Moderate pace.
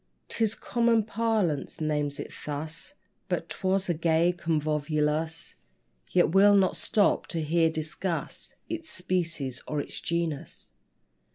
No: slow, 120 wpm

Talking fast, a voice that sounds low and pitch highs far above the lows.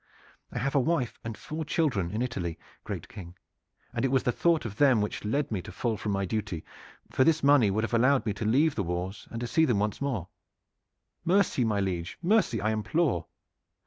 Yes: fast, 210 wpm; low, 115 Hz; wide, 5.7 semitones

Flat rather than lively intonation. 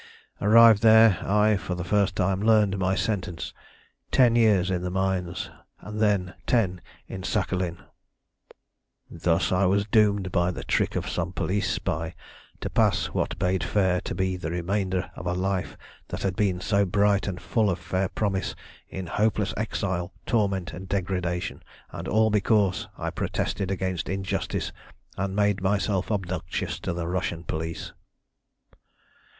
Yes: narrow, 2.3 semitones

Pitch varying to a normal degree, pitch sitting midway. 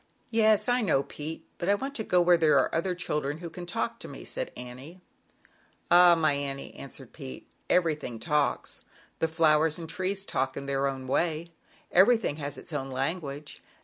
Yes: average, 4.3 semitones; medium, 160 Hz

